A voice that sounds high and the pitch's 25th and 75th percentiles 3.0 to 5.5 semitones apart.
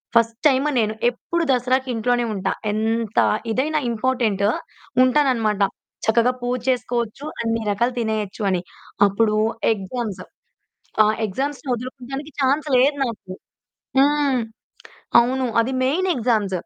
Yes: high, 240 Hz; average, 3.3 semitones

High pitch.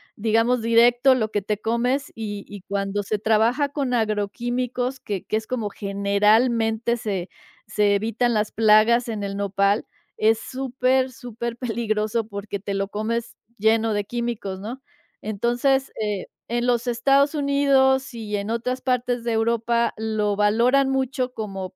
Yes: high, 225 Hz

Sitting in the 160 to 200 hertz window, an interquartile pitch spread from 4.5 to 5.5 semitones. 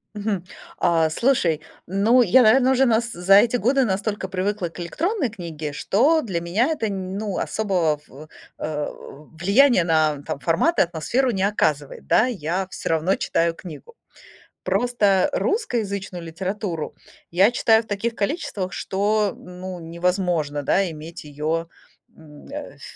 Yes: high, 190 Hz; average, 5.2 semitones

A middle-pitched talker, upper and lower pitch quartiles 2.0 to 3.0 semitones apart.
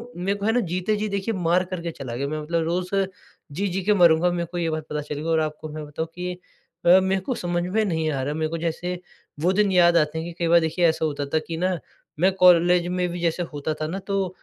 Yes: medium, 175 Hz; narrow, 2.4 semitones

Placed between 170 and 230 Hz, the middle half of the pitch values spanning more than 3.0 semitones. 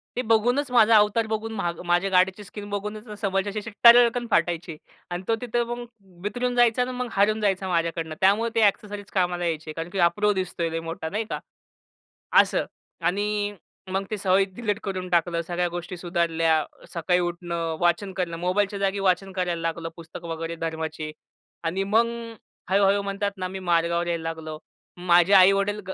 Yes: high, 190 Hz; average, 3.6 semitones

